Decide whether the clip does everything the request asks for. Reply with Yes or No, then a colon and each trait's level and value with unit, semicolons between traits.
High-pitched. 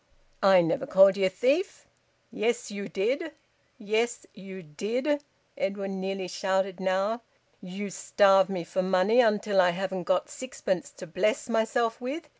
Yes: high, 195 Hz